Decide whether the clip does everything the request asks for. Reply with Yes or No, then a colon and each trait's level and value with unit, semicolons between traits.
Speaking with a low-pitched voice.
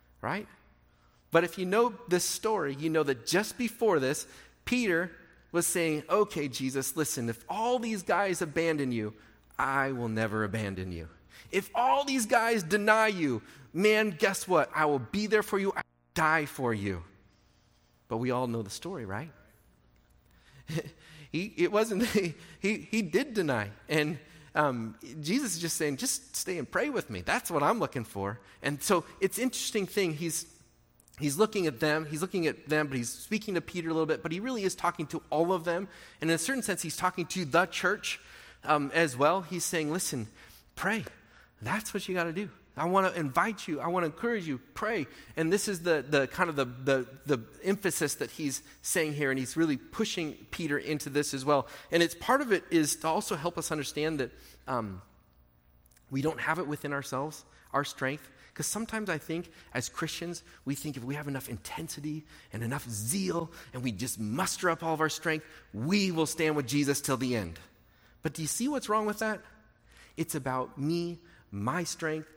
No: medium, 155 Hz